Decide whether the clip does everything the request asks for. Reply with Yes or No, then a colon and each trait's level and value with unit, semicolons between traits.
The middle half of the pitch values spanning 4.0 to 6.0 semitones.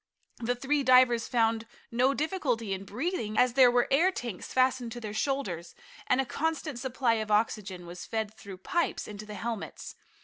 No: average, 3.6 semitones